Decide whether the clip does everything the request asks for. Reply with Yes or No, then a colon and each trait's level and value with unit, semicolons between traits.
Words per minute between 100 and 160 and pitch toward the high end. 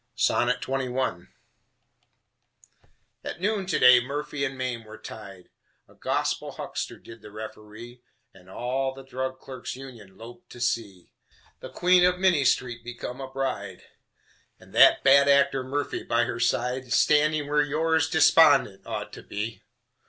No: average, 145 wpm; low, 130 Hz